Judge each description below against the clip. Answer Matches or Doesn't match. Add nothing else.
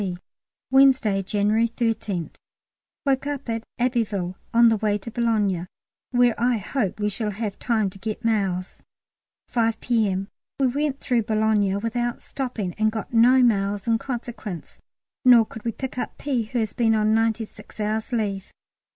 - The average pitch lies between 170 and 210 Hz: Doesn't match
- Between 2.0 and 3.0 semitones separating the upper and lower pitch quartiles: Matches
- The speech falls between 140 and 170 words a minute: Matches